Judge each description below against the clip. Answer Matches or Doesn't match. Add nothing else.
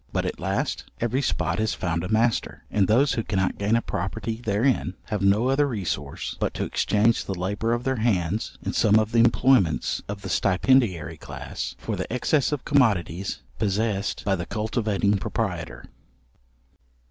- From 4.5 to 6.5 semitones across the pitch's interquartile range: Doesn't match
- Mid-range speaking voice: Doesn't match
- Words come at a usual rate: Matches